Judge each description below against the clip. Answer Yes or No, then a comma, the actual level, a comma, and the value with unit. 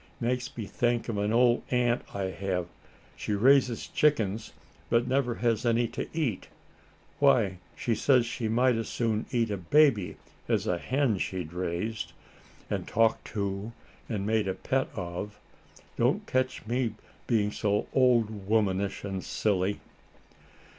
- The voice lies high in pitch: No, low, 110 Hz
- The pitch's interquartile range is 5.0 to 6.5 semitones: No, average, 3.5 semitones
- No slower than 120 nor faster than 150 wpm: Yes, average, 145 wpm